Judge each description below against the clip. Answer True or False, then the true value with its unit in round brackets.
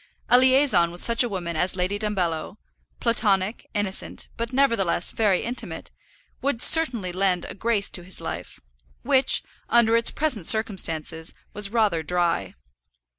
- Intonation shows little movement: False (4.6 semitones)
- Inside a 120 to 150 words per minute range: True (140 wpm)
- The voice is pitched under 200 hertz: False (205 Hz)